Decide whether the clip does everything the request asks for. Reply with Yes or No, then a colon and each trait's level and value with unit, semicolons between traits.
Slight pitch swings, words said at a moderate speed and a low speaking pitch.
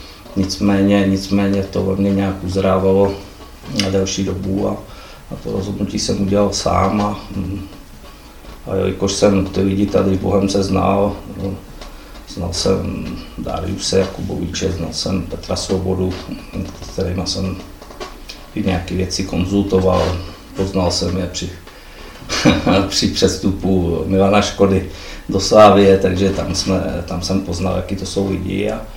Yes: narrow, 1.1 semitones; average, 130 wpm; very low, 95 Hz